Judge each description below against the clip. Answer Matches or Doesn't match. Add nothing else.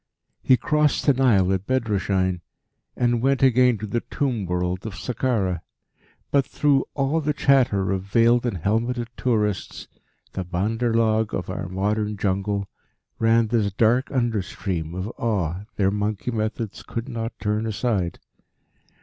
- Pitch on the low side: Matches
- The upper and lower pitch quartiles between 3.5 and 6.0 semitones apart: Matches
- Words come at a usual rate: Matches